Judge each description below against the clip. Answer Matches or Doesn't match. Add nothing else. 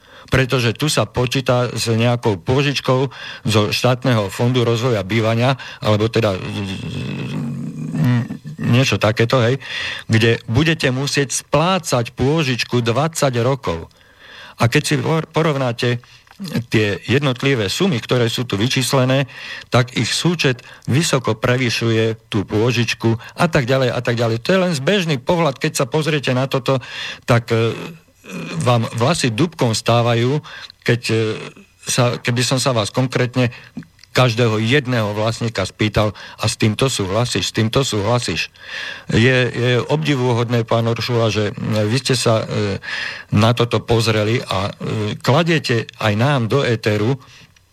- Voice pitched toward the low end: Matches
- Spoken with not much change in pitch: Doesn't match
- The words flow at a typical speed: Matches